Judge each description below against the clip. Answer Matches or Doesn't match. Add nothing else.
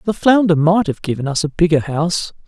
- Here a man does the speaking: Matches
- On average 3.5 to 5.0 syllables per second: Doesn't match